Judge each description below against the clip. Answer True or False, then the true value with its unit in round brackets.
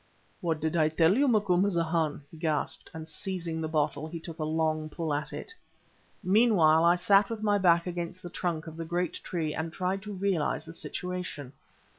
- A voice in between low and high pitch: True (165 Hz)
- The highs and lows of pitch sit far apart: False (2.6 semitones)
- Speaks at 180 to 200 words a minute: True (190 wpm)